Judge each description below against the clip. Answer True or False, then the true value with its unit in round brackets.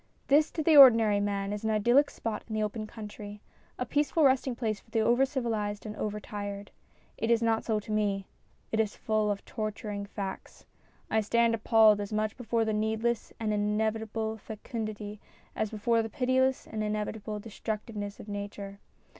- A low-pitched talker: False (215 Hz)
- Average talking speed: True (175 wpm)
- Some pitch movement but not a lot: False (1.7 semitones)